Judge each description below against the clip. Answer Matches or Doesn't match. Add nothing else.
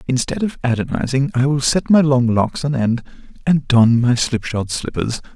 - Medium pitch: Doesn't match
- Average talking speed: Matches